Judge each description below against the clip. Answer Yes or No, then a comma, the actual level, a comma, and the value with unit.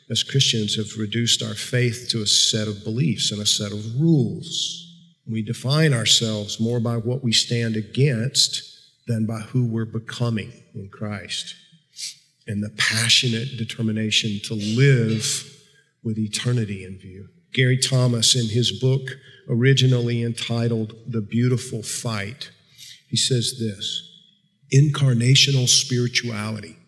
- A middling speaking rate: No, slow, 125 wpm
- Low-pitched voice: Yes, low, 120 Hz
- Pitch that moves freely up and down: No, average, 3.5 semitones